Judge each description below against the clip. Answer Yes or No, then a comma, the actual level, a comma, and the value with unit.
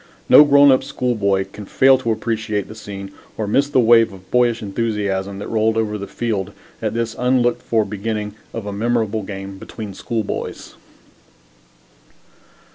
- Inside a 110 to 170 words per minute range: Yes, average, 155 wpm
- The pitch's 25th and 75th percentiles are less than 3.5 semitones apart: Yes, average, 2.8 semitones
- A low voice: Yes, low, 110 Hz